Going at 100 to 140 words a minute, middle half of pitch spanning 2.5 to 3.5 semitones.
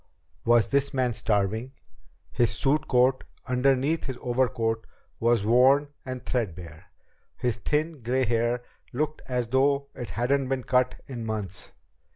Yes: slow, 135 wpm; average, 2.8 semitones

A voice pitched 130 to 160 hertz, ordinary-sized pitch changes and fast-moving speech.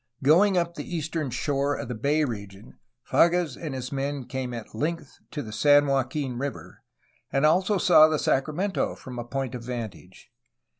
No: medium, 140 Hz; average, 3.9 semitones; average, 170 wpm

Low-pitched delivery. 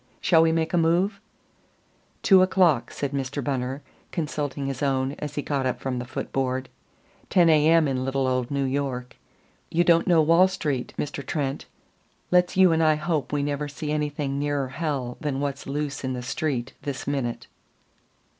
No: medium, 145 Hz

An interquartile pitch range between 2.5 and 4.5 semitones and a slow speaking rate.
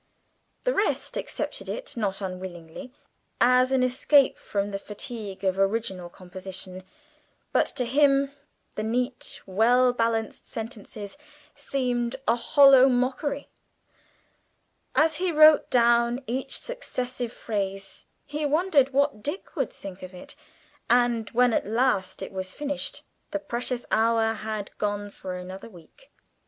No: average, 5.2 semitones; slow, 130 wpm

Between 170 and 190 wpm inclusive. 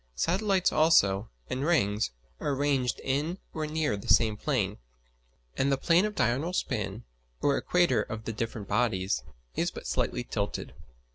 No: average, 150 wpm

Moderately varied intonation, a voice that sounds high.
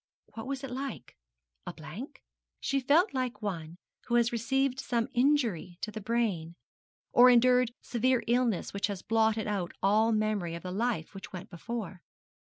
Yes: average, 4.1 semitones; high, 225 Hz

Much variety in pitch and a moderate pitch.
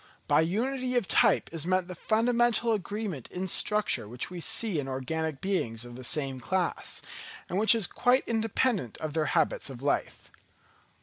Yes: wide, 7.6 semitones; medium, 180 Hz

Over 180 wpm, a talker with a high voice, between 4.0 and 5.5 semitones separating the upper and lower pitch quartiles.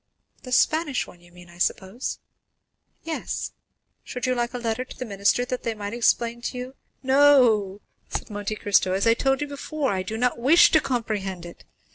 Yes: average, 195 wpm; high, 235 Hz; average, 4.3 semitones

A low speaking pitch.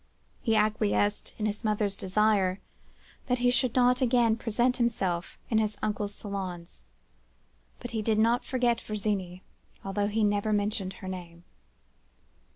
No: high, 210 Hz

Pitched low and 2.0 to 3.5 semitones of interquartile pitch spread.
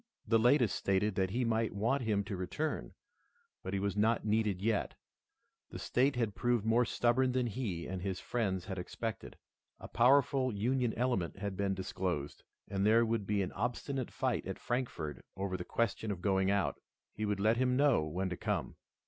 No: low, 105 Hz; average, 4.0 semitones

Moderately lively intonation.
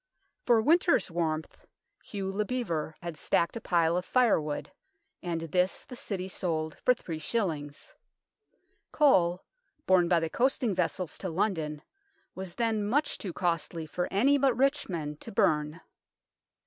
No: wide, 5.7 semitones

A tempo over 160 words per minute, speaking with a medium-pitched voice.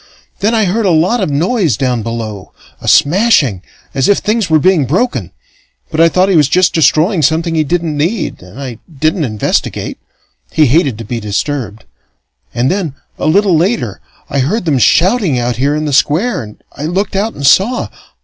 Yes: average, 190 wpm; medium, 155 Hz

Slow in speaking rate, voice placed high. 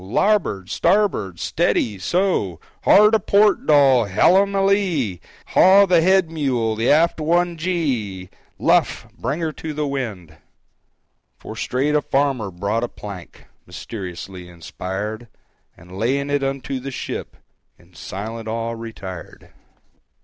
No: slow, 120 wpm; low, 130 Hz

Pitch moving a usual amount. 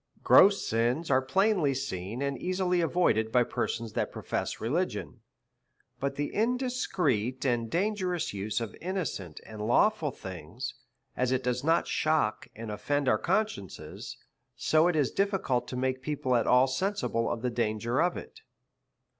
No: wide, 7.4 semitones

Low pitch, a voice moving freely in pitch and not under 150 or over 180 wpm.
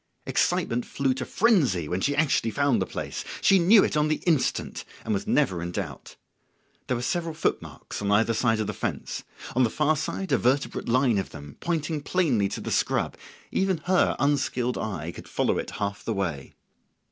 No: low, 125 Hz; wide, 7.3 semitones; average, 195 wpm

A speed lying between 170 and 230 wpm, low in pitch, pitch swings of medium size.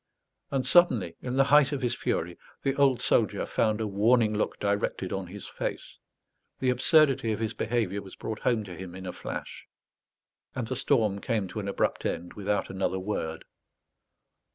Yes: average, 175 wpm; low, 110 Hz; average, 4.5 semitones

